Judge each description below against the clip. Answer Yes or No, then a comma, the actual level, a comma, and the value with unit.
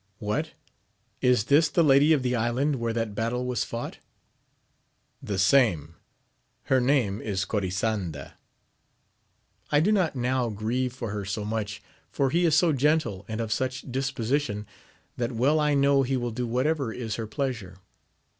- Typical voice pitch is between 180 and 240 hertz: No, low, 125 Hz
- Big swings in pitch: No, average, 4.4 semitones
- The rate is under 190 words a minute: Yes, average, 170 wpm